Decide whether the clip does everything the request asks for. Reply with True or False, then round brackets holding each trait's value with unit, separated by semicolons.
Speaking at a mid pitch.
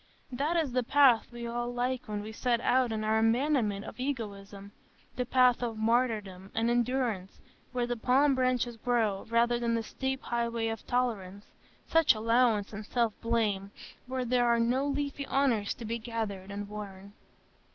False (235 Hz)